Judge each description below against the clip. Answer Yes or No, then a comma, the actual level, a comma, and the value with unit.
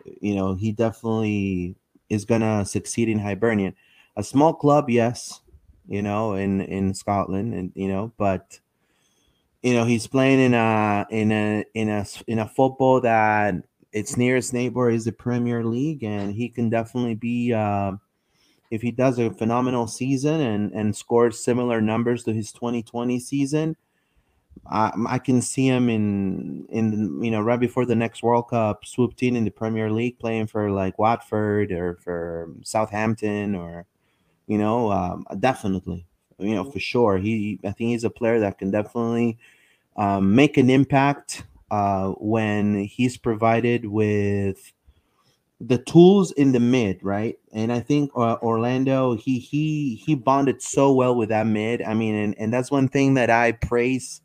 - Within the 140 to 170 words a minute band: Yes, average, 165 wpm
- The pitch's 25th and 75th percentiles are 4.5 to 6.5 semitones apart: No, average, 2.9 semitones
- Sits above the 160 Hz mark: No, low, 115 Hz